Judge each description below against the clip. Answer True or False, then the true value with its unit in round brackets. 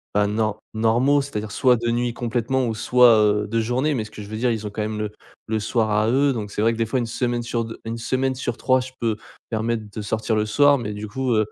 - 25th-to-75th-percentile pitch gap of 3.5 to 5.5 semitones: False (2.5 semitones)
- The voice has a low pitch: True (115 Hz)